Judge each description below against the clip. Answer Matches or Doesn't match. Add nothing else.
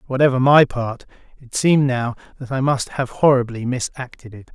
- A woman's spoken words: Doesn't match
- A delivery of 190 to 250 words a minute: Doesn't match